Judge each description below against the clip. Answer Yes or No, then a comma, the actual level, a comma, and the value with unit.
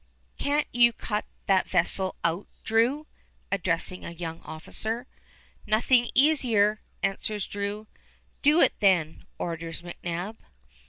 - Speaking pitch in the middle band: No, high, 205 Hz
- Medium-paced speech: No, slow, 110 wpm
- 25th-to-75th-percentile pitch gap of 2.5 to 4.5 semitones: No, average, 5.2 semitones